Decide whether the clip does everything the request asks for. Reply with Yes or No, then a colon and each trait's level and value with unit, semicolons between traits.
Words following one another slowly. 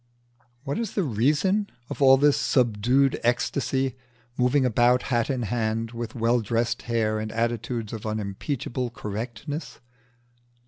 Yes: slow, 130 wpm